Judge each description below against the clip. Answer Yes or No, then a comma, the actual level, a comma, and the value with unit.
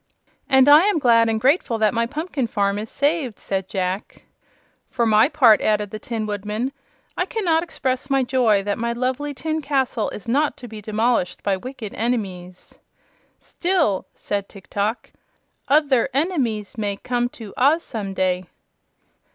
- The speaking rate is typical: Yes, average, 165 wpm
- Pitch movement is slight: No, average, 4.8 semitones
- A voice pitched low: No, high, 235 Hz